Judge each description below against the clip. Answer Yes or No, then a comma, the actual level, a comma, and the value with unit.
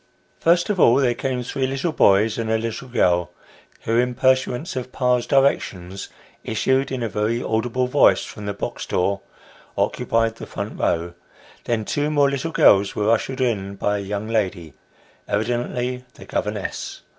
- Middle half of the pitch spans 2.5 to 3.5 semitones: No, average, 4.1 semitones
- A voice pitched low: Yes, low, 120 Hz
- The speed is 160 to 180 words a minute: Yes, average, 165 wpm